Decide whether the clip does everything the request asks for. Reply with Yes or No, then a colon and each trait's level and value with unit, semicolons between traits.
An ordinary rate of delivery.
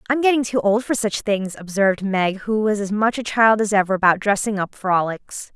No: fast, 225 wpm